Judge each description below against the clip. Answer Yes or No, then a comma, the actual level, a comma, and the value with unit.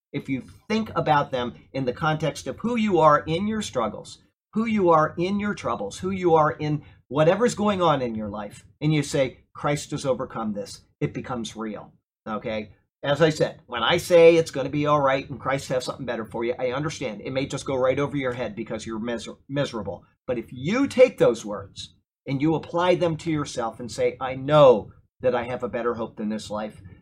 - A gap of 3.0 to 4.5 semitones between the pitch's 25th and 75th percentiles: No, wide, 5.6 semitones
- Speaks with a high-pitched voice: No, low, 135 Hz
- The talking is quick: Yes, fast, 220 wpm